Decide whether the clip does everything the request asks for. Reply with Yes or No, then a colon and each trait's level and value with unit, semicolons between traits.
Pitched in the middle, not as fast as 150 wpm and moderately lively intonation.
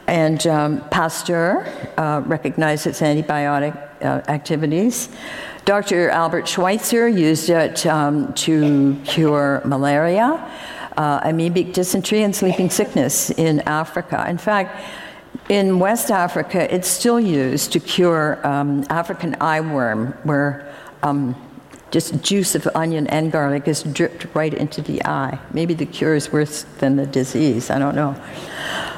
Yes: medium, 160 Hz; slow, 135 wpm; average, 3.8 semitones